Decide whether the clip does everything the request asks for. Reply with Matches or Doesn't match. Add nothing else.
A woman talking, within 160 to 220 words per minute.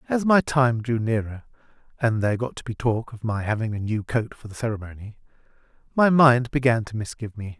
Doesn't match